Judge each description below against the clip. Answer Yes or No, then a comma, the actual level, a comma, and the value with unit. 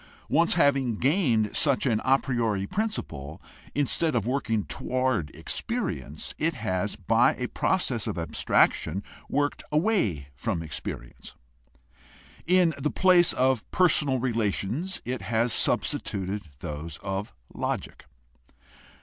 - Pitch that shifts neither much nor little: No, wide, 6.9 semitones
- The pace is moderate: No, slow, 115 wpm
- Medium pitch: No, low, 120 Hz